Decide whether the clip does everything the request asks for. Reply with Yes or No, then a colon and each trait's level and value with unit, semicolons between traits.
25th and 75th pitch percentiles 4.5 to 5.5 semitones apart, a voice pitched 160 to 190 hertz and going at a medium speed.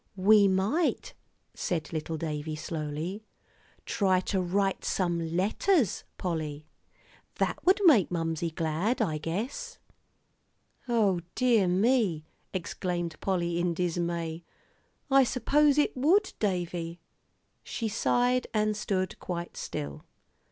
No: average, 5.2 semitones; medium, 185 Hz; slow, 110 wpm